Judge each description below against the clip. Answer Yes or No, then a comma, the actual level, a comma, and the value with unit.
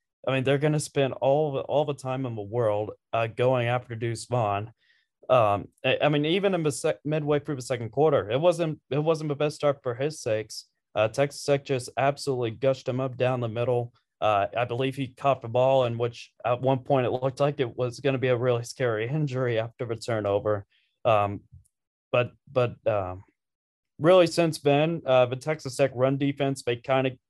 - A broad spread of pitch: No, average, 3.1 semitones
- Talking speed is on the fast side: Yes, fast, 210 wpm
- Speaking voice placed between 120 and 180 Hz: Yes, low, 130 Hz